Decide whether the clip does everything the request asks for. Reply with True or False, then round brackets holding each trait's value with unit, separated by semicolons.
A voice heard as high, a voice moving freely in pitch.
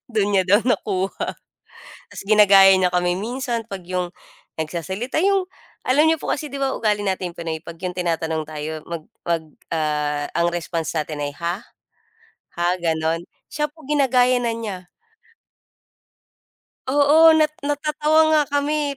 True (195 Hz; 8.5 semitones)